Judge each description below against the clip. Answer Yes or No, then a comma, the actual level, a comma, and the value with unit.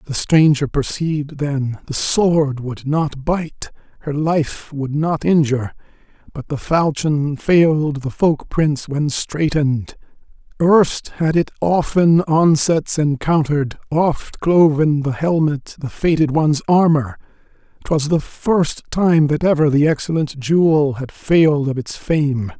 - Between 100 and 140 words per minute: Yes, slow, 135 wpm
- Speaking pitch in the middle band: Yes, medium, 150 Hz